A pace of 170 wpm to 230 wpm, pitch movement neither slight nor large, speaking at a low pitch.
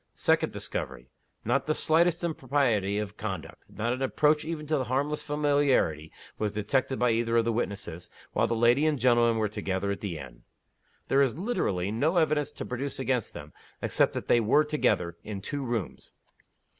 No: average, 180 wpm; wide, 5.8 semitones; low, 120 Hz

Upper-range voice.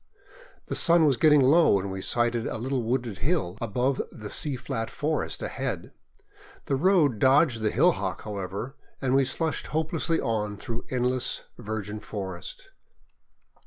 No: low, 125 Hz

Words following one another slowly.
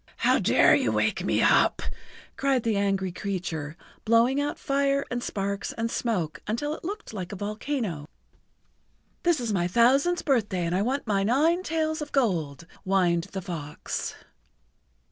No: average, 155 wpm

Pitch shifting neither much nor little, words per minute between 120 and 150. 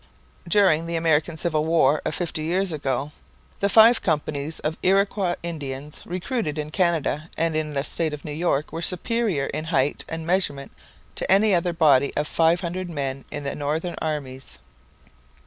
No: average, 3.1 semitones; average, 165 wpm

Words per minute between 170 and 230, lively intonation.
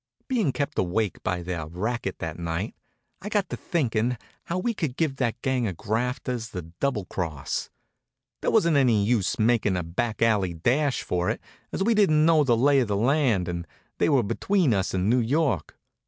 Yes: average, 195 wpm; wide, 7.2 semitones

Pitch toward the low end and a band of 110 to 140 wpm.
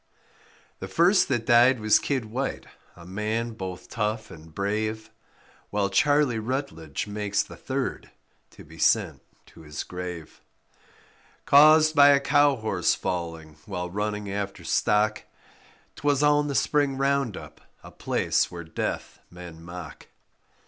Yes: low, 110 Hz; slow, 135 wpm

